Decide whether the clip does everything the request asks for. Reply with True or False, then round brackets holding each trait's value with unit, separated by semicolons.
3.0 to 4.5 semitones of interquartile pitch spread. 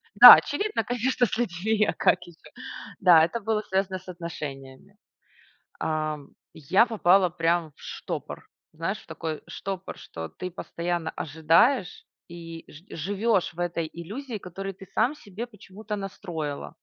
True (4.2 semitones)